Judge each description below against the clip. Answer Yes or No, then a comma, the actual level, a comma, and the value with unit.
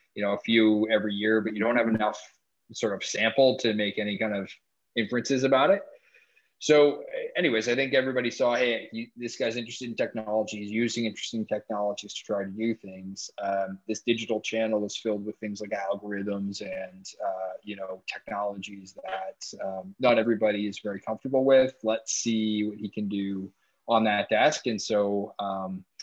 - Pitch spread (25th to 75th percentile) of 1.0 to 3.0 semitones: Yes, narrow, 2.5 semitones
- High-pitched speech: No, low, 110 Hz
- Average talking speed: Yes, average, 180 wpm